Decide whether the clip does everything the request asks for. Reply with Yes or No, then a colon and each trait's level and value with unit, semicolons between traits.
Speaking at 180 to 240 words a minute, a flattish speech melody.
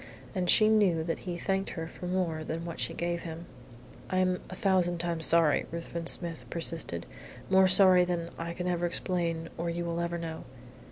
Yes: average, 190 wpm; narrow, 1.5 semitones